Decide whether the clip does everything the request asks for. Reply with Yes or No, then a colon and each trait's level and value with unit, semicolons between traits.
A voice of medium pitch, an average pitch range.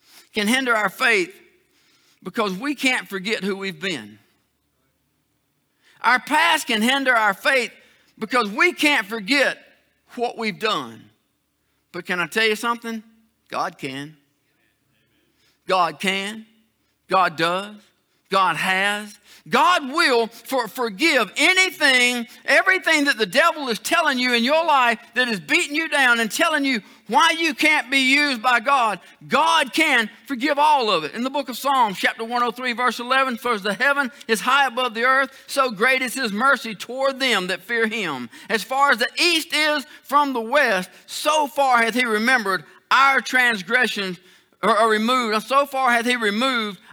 No: very high, 250 Hz; average, 4.6 semitones